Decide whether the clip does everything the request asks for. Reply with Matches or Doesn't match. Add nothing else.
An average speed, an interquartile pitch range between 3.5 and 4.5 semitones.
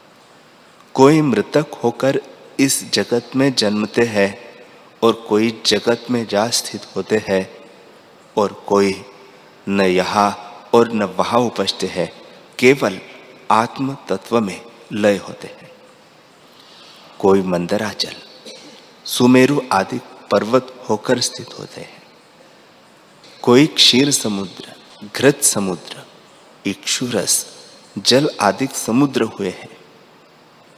Doesn't match